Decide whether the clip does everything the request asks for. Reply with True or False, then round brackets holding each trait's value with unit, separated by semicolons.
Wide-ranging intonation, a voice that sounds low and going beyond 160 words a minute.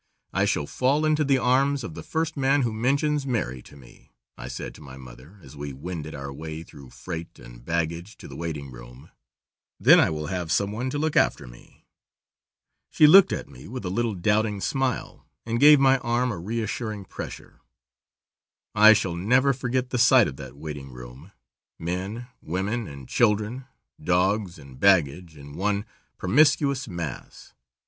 True (8.7 semitones; 100 Hz; 170 wpm)